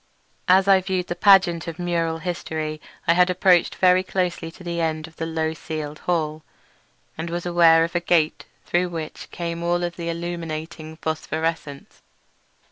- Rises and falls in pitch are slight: Yes, narrow, 1.7 semitones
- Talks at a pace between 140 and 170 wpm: Yes, average, 165 wpm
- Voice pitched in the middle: Yes, medium, 170 Hz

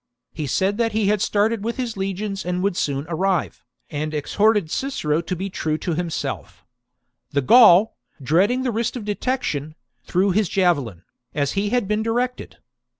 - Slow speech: No, average, 165 wpm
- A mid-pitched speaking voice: No, high, 195 Hz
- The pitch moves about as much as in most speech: No, wide, 5.7 semitones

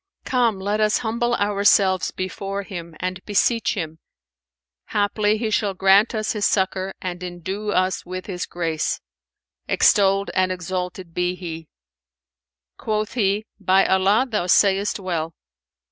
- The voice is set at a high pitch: Yes, high, 195 Hz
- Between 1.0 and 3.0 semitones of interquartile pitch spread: Yes, narrow, 2.4 semitones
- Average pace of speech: No, slow, 130 wpm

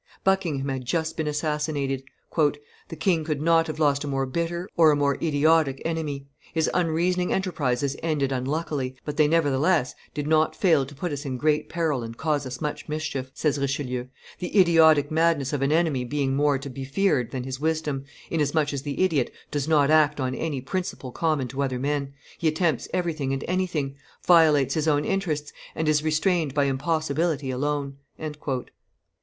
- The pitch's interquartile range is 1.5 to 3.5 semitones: Yes, average, 2.8 semitones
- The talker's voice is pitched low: No, medium, 150 Hz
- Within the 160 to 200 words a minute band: Yes, average, 175 wpm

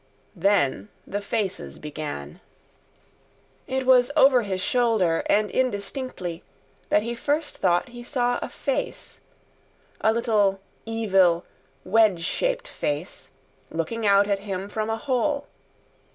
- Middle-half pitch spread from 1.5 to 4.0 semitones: No, average, 4.9 semitones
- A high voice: Yes, high, 210 Hz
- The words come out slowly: Yes, slow, 120 wpm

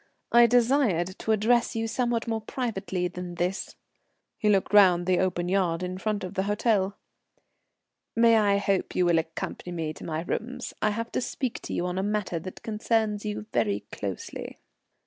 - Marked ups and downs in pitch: No, average, 4.0 semitones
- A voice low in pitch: No, high, 200 Hz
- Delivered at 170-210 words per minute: Yes, average, 180 wpm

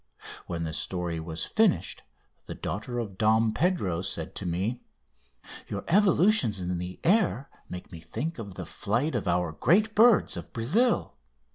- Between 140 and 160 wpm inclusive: Yes, average, 155 wpm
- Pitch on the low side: Yes, low, 110 Hz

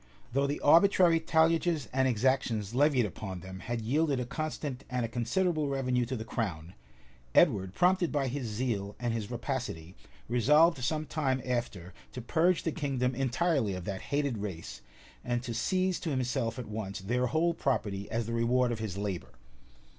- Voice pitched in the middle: No, low, 125 Hz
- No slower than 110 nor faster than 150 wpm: No, average, 170 wpm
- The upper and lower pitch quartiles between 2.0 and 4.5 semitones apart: No, average, 5.0 semitones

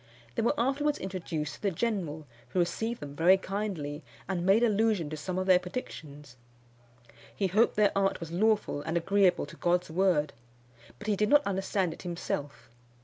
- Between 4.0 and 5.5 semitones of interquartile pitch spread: Yes, average, 4.4 semitones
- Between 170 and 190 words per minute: Yes, average, 175 wpm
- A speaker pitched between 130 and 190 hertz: Yes, medium, 185 Hz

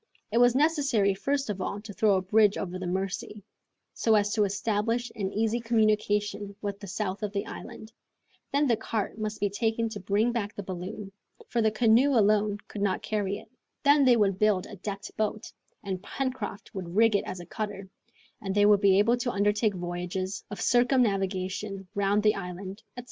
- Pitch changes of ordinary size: No, narrow, 2.2 semitones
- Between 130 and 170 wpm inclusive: No, average, 190 wpm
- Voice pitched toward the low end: No, high, 205 Hz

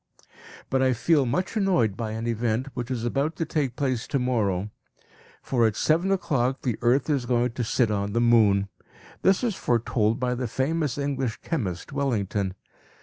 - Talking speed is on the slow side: No, average, 170 wpm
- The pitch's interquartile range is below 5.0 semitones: Yes, average, 3.9 semitones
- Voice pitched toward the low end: Yes, low, 125 Hz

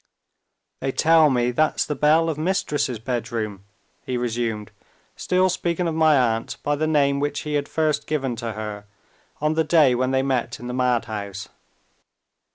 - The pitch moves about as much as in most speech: Yes, average, 4.6 semitones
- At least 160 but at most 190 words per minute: Yes, average, 165 wpm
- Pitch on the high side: No, low, 135 Hz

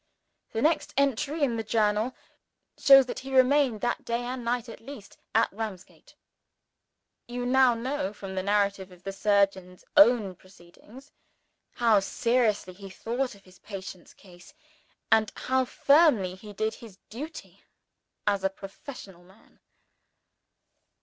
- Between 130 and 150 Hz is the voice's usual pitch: No, high, 220 Hz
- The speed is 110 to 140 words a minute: Yes, slow, 135 wpm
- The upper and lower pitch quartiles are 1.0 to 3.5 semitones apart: No, average, 4.5 semitones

